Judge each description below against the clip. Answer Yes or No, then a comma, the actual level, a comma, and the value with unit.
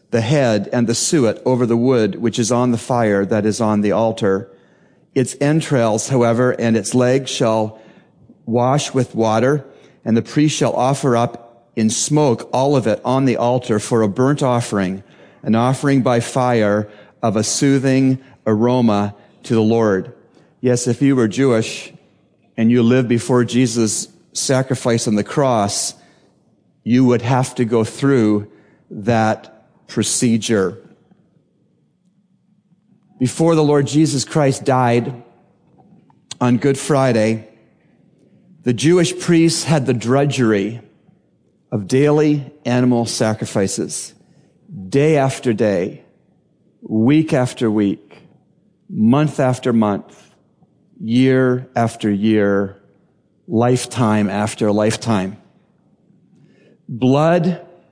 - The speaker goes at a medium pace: No, slow, 120 wpm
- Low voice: Yes, low, 125 Hz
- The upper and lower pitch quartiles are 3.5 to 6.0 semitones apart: Yes, average, 3.9 semitones